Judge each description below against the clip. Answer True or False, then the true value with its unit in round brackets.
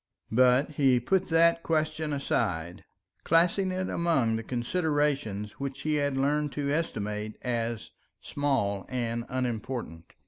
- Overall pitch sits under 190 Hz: True (135 Hz)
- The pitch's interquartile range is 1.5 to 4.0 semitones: False (5.1 semitones)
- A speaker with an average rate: False (125 wpm)